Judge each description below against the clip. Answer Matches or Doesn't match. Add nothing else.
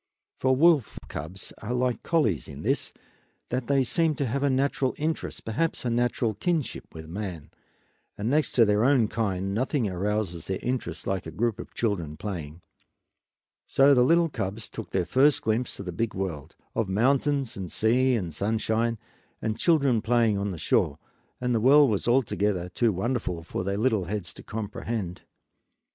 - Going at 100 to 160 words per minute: Doesn't match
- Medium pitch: Doesn't match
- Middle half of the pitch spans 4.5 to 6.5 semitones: Matches